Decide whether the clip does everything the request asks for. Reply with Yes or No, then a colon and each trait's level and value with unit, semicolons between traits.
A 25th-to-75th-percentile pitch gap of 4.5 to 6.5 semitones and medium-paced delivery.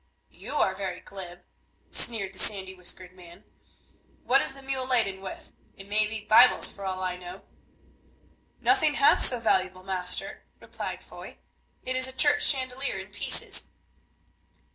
Yes: wide, 5.6 semitones; average, 150 wpm